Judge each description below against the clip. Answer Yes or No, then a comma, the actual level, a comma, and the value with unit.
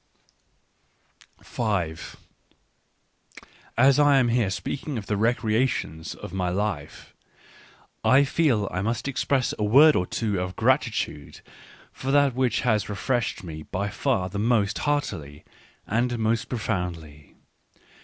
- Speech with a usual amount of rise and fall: No, wide, 5.7 semitones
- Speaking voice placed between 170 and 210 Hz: No, low, 110 Hz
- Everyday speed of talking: No, slow, 125 wpm